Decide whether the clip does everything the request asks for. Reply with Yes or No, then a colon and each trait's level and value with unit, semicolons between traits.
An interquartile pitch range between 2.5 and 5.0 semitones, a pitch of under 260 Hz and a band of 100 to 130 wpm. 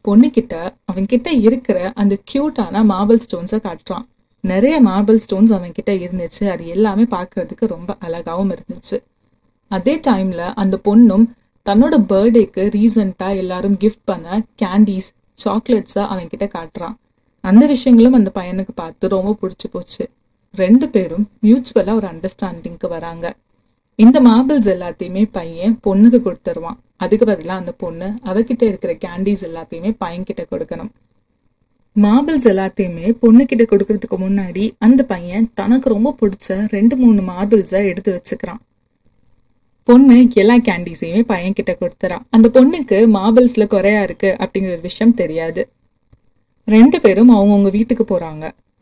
Yes: average, 3.6 semitones; high, 205 Hz; average, 115 wpm